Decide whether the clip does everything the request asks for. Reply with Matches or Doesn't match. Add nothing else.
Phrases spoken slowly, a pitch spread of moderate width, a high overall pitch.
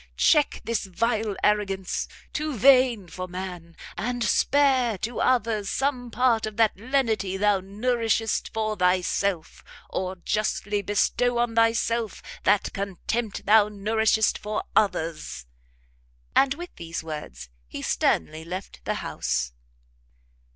Matches